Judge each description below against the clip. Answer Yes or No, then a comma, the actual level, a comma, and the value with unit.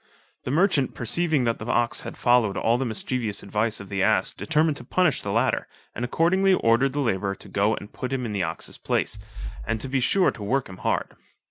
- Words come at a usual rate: No, fast, 220 wpm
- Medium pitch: No, low, 120 Hz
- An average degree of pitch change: Yes, average, 4.7 semitones